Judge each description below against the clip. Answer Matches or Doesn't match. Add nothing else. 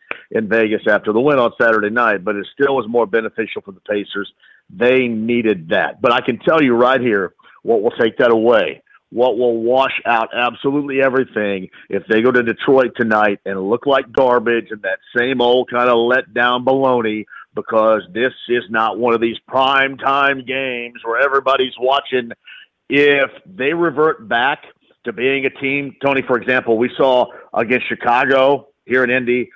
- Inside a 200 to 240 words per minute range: Doesn't match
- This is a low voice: Matches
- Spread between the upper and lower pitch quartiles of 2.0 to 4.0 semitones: Matches